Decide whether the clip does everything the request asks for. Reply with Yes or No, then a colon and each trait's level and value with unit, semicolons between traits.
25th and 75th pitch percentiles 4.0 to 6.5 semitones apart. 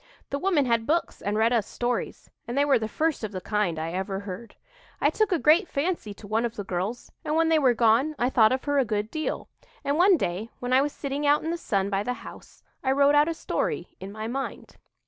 Yes: wide, 5.5 semitones